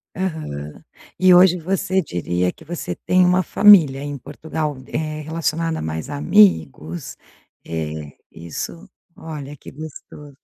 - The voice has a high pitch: No, medium, 150 Hz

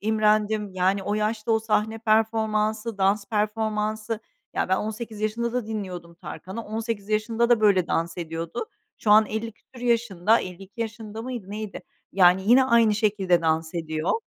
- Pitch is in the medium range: No, high, 215 Hz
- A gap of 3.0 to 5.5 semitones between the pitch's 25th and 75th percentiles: No, narrow, 2.4 semitones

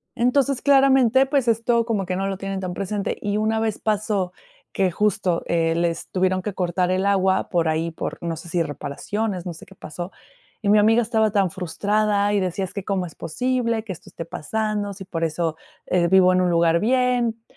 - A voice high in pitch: Yes, high, 195 Hz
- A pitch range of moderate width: Yes, average, 3.7 semitones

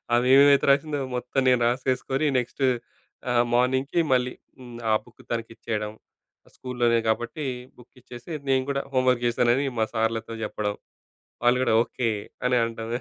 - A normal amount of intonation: No, narrow, 2.0 semitones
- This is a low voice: Yes, low, 125 Hz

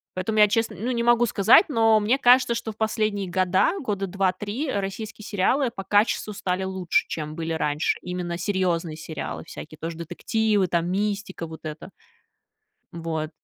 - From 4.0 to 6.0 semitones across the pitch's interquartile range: Yes, average, 4.3 semitones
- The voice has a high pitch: Yes, high, 195 Hz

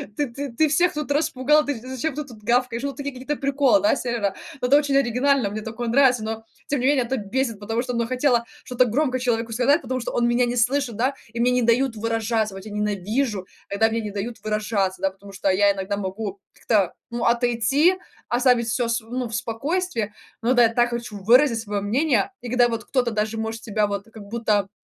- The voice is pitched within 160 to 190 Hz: No, high, 235 Hz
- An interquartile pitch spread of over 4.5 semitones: No, average, 3.2 semitones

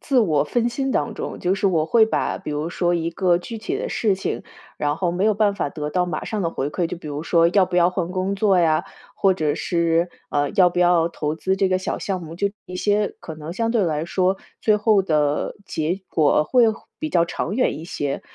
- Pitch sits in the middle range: Yes, medium, 180 Hz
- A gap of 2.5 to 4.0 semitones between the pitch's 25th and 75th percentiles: Yes, average, 3.7 semitones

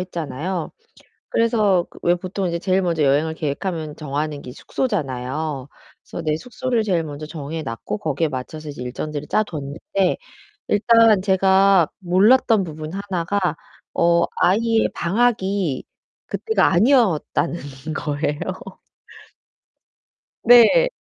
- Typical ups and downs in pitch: Yes, average, 5.0 semitones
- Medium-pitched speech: Yes, medium, 170 Hz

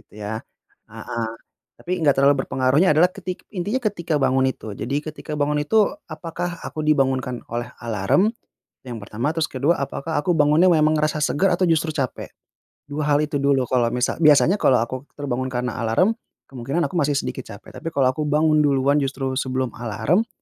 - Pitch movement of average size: Yes, average, 3.7 semitones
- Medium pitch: Yes, medium, 145 Hz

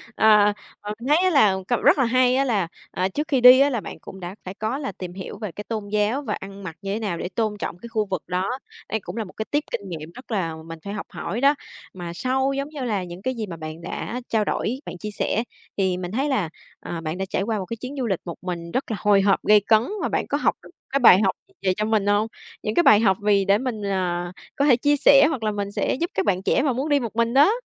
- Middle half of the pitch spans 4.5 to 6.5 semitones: Yes, average, 5.0 semitones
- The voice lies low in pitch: No, high, 210 Hz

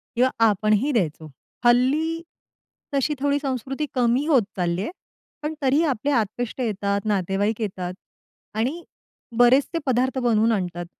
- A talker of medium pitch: No, high, 240 Hz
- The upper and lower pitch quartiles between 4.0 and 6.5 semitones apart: Yes, average, 5.1 semitones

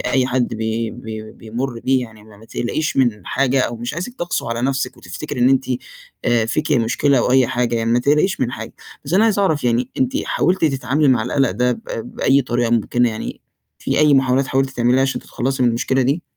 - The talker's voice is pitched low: Yes, low, 125 Hz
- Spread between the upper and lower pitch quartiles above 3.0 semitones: No, narrow, 2.6 semitones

